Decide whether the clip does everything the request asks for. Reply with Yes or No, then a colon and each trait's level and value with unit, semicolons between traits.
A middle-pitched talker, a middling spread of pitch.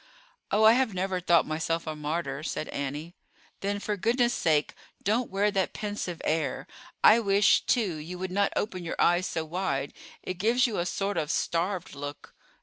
Yes: medium, 180 Hz; average, 4.2 semitones